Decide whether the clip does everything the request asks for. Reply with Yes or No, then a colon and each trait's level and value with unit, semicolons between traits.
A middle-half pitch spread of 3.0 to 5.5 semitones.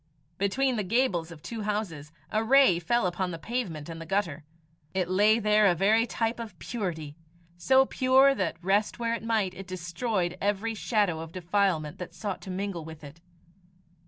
Yes: average, 4.7 semitones